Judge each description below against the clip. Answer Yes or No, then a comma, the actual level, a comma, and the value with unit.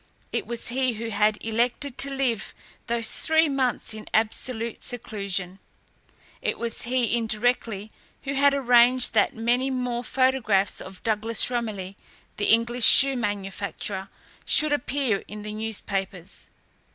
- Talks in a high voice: Yes, high, 230 Hz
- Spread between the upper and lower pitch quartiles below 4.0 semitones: Yes, average, 3.2 semitones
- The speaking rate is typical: No, slow, 130 wpm